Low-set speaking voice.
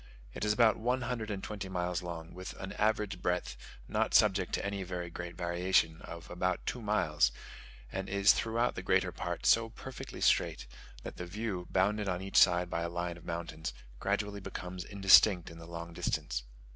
Yes: very low, 95 Hz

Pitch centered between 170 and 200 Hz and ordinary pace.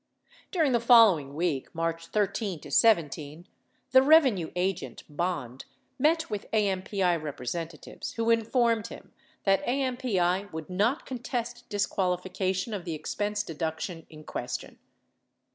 No: high, 190 Hz; slow, 115 wpm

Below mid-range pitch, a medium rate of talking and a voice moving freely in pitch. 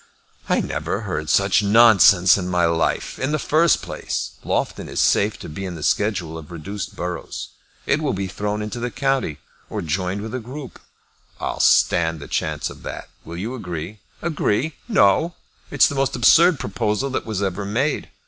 Yes: low, 100 Hz; average, 180 wpm; wide, 6.3 semitones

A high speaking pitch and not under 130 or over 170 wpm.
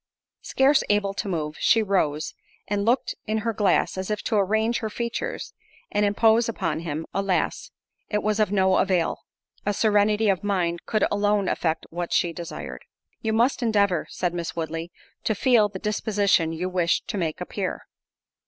Yes: high, 200 Hz; average, 165 wpm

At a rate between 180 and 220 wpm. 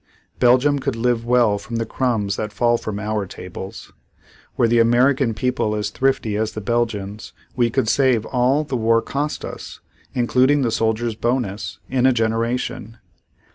No: average, 160 wpm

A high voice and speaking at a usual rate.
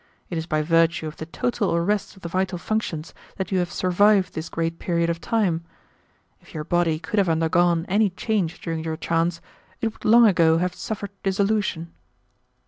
No: medium, 175 Hz; average, 185 wpm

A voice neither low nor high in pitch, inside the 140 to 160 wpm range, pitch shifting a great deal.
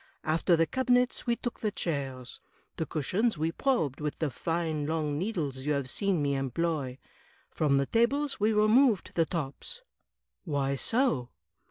Yes: medium, 165 Hz; average, 155 wpm; wide, 7.7 semitones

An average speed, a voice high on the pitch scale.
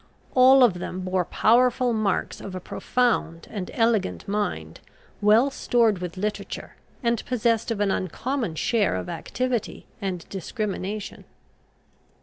No: slow, 130 wpm; high, 210 Hz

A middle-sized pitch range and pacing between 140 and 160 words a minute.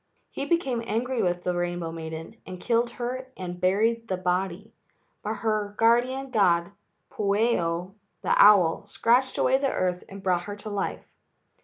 Yes: average, 4.7 semitones; average, 155 wpm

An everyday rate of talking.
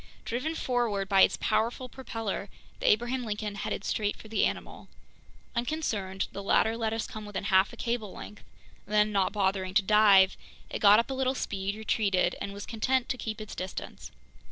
Yes: average, 180 wpm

